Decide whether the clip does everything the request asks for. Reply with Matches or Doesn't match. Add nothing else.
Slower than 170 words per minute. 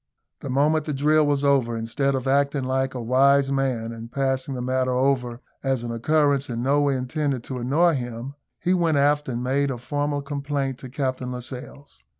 Doesn't match